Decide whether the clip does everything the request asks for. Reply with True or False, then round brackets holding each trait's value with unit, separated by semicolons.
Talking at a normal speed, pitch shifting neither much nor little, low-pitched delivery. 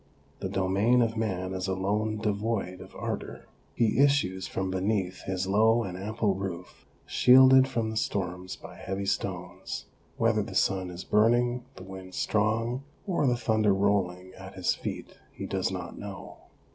True (160 wpm; 3.2 semitones; 100 Hz)